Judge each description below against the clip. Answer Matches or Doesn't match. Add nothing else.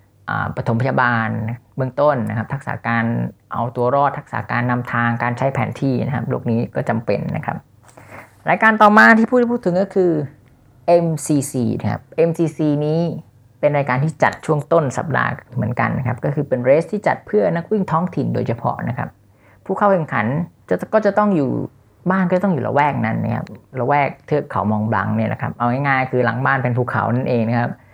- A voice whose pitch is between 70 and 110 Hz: Doesn't match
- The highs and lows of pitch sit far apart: Matches